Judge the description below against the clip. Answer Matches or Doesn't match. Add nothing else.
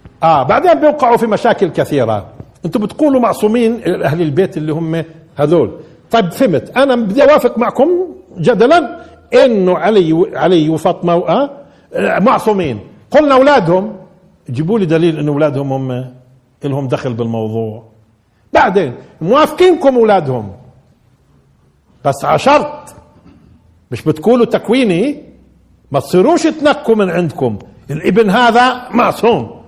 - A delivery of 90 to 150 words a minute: Matches